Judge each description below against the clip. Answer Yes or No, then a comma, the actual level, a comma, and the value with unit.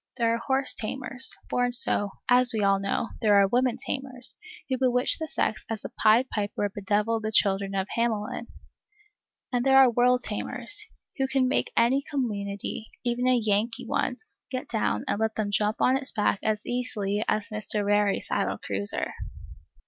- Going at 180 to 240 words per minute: No, average, 170 wpm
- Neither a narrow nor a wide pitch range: Yes, average, 3.3 semitones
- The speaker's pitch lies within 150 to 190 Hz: No, high, 230 Hz